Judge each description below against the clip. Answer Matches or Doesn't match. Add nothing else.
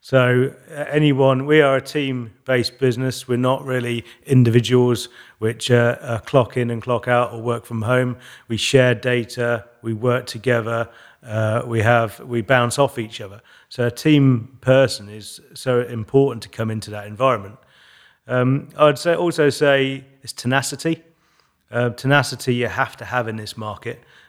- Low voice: Matches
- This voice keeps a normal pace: Matches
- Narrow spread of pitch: Matches